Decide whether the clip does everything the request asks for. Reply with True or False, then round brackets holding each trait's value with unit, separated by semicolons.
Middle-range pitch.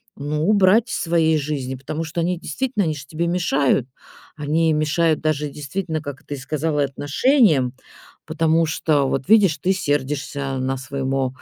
True (150 Hz)